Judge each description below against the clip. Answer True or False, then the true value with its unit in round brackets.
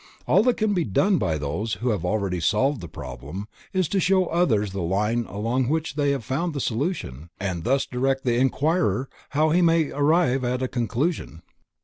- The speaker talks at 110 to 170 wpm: False (205 wpm)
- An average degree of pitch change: False (7.7 semitones)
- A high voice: False (130 Hz)